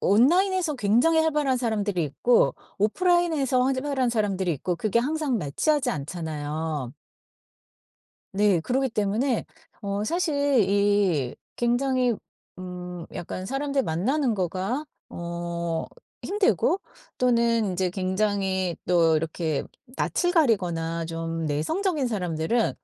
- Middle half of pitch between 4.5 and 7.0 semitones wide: No, wide, 7.5 semitones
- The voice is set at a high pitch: Yes, high, 210 Hz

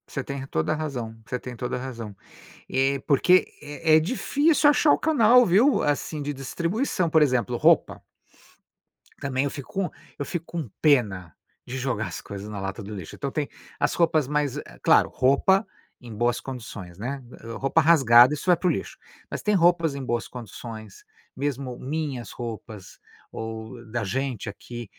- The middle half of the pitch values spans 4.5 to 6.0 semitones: Yes, average, 5.1 semitones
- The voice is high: No, low, 135 Hz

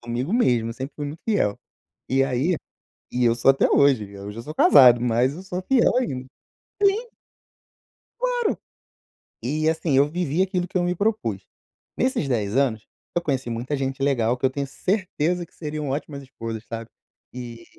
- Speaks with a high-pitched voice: No, low, 135 Hz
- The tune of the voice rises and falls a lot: Yes, wide, 6.5 semitones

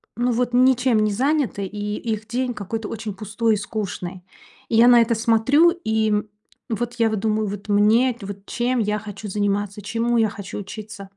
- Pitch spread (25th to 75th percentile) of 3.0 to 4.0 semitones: No, narrow, 2.6 semitones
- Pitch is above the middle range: Yes, high, 220 Hz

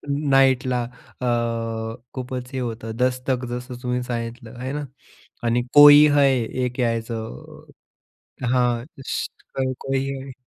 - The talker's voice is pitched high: No, low, 125 Hz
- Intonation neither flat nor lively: No, narrow, 1.9 semitones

